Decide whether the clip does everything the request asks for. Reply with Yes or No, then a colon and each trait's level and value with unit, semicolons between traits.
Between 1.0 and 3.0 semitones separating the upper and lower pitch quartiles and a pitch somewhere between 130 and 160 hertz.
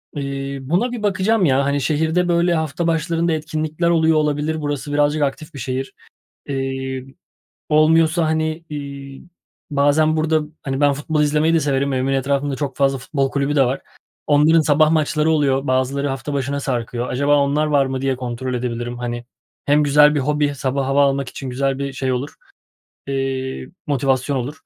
Yes: narrow, 2.5 semitones; medium, 140 Hz